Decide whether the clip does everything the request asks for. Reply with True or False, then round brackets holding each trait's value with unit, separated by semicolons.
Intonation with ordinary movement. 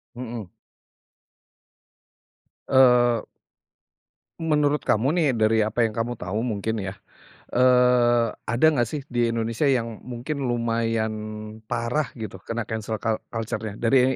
False (2.1 semitones)